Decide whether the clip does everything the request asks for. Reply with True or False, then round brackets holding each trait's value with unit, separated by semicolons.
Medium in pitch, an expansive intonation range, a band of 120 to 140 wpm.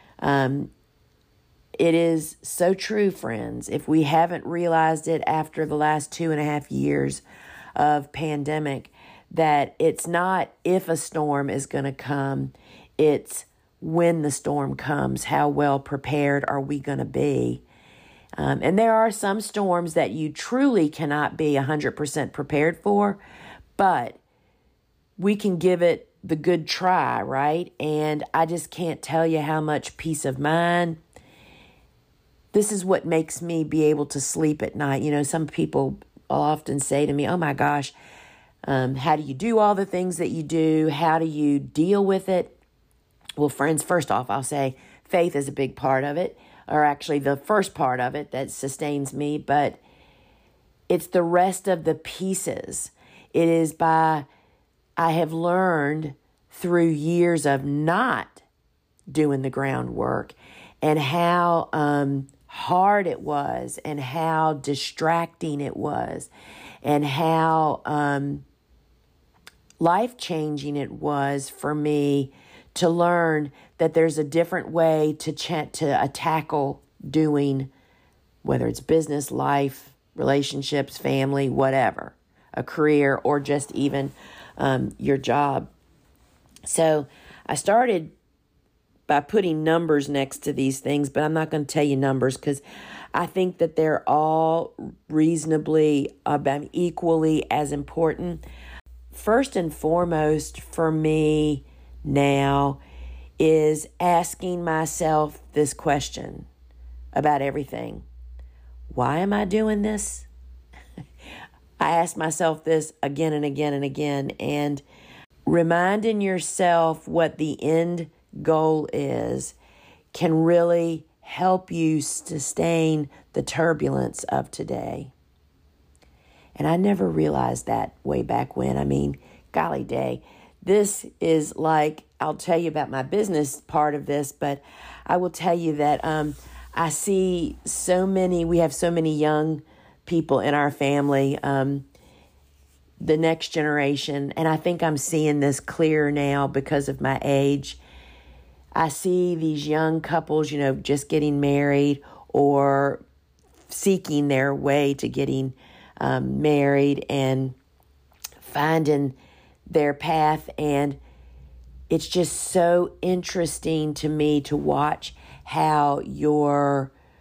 False (150 Hz; 2.9 semitones; 135 wpm)